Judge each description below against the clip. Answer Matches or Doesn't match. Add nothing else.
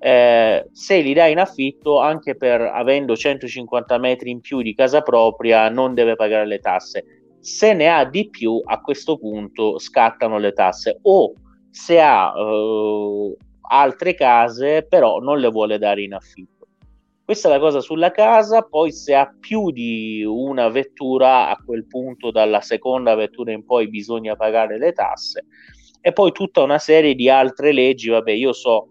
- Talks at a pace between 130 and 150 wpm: Doesn't match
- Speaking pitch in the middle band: Doesn't match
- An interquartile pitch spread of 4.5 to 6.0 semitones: Matches